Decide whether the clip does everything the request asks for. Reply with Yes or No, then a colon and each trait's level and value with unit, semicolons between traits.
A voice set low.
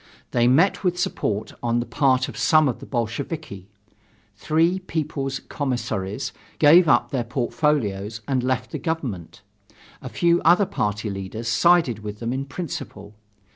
Yes: low, 130 Hz